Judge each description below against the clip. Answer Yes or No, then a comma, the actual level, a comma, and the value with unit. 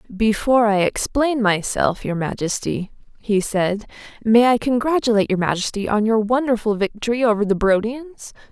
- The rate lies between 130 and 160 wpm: Yes, average, 140 wpm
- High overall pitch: Yes, high, 220 Hz